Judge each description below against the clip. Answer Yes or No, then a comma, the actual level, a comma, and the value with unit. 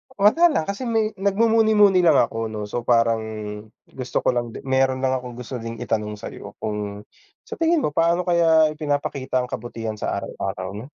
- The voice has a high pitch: No, low, 130 Hz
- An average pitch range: No, wide, 8.3 semitones